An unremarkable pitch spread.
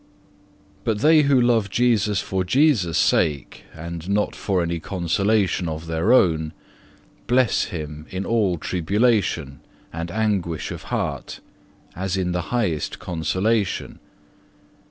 Yes: average, 4.9 semitones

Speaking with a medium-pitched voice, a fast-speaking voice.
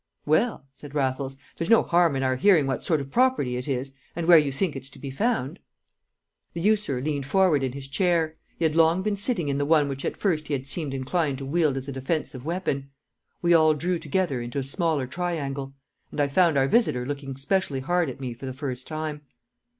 Yes: medium, 145 Hz; fast, 220 wpm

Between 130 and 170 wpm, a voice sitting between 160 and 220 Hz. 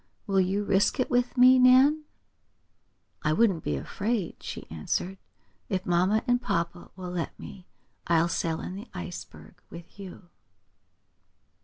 Yes: average, 145 wpm; high, 190 Hz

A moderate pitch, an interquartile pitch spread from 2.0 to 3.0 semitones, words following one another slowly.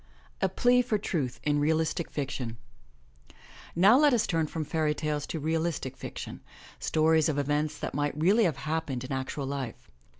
No: medium, 155 Hz; narrow, 2.6 semitones; average, 165 wpm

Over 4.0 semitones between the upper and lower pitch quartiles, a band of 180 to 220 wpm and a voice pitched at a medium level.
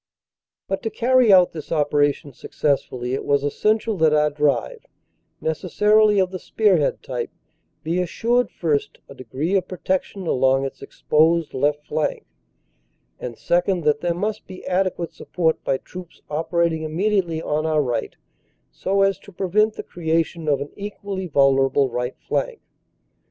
No: average, 4.8 semitones; average, 150 wpm; medium, 165 Hz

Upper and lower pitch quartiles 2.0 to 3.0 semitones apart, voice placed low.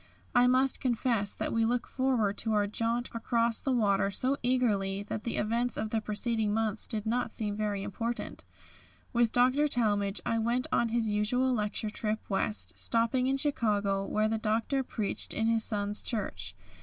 No: average, 2.7 semitones; high, 225 Hz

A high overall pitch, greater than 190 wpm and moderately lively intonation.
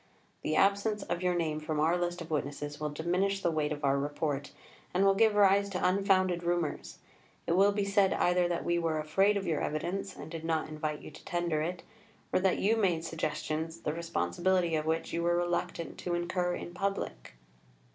No: medium, 175 Hz; average, 200 wpm; average, 3.2 semitones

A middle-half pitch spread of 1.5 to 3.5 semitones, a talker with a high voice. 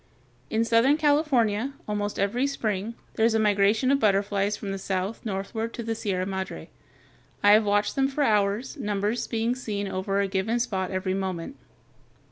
Yes: average, 3.0 semitones; high, 210 Hz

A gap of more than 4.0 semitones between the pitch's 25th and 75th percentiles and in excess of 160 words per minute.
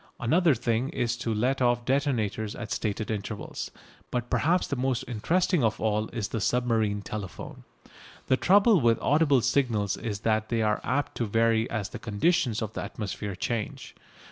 No: average, 3.4 semitones; average, 170 wpm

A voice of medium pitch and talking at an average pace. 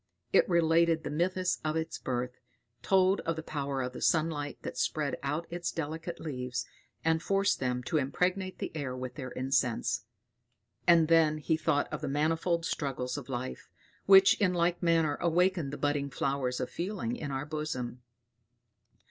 Yes: medium, 155 Hz; average, 170 wpm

